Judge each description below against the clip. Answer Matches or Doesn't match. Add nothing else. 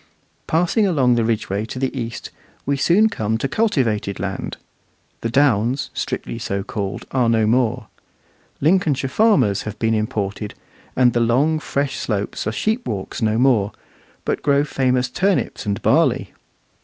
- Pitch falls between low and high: Doesn't match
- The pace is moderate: Matches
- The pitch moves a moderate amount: Matches